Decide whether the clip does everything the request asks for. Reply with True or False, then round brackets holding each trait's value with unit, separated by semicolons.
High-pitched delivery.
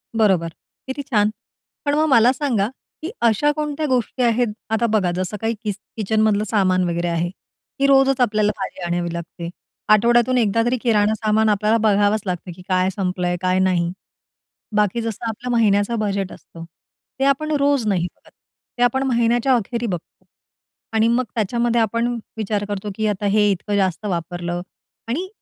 True (215 Hz)